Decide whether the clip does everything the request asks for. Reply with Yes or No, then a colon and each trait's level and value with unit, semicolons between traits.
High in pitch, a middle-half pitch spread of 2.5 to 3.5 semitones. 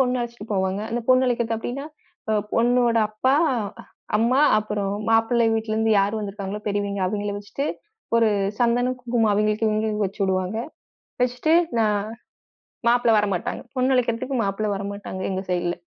Yes: high, 220 Hz; average, 3.0 semitones